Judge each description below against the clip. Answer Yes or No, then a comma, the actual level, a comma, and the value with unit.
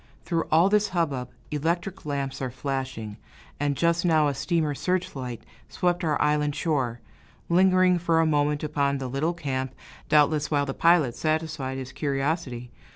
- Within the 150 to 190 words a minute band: Yes, average, 155 wpm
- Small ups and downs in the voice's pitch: No, average, 3.6 semitones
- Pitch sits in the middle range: Yes, medium, 150 Hz